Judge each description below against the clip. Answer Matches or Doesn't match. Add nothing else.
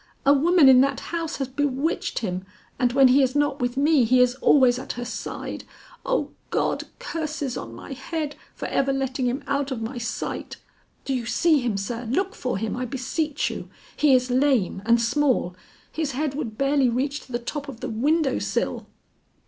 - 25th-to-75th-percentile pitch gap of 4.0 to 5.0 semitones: Doesn't match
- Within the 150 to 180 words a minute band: Doesn't match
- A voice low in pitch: Doesn't match